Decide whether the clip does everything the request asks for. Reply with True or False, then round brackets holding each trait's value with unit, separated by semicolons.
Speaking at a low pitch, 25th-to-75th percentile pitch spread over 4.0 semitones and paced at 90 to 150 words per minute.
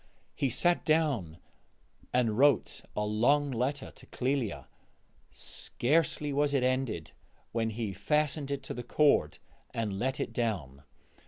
True (125 Hz; 4.9 semitones; 135 wpm)